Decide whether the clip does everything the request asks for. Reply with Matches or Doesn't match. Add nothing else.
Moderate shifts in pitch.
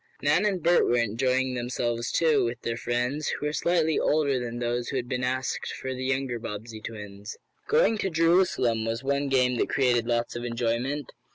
Matches